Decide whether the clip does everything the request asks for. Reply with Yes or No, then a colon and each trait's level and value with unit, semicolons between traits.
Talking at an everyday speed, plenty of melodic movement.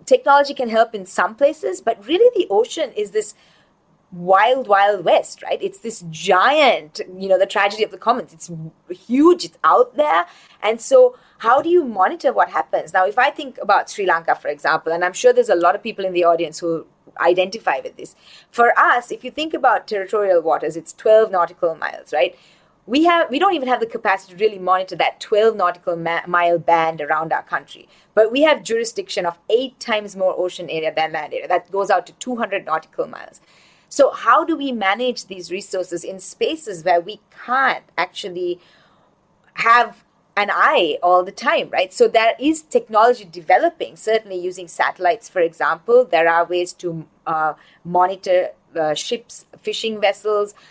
Yes: average, 185 wpm; wide, 6.4 semitones